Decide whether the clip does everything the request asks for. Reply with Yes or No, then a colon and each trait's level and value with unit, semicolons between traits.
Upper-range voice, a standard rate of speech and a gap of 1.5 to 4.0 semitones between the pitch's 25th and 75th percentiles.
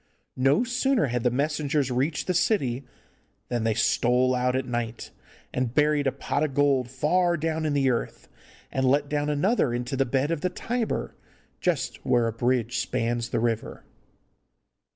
No: low, 135 Hz; average, 170 wpm; average, 3.7 semitones